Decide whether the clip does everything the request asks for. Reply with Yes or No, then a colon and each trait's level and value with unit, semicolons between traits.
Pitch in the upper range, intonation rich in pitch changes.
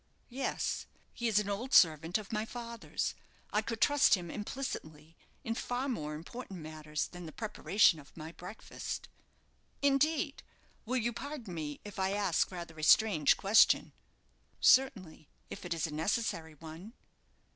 Yes: high, 195 Hz; wide, 6.5 semitones